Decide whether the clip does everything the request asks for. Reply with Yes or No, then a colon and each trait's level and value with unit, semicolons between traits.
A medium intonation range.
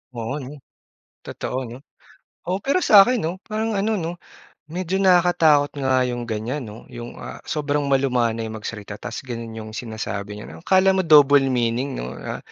No: wide, 7.4 semitones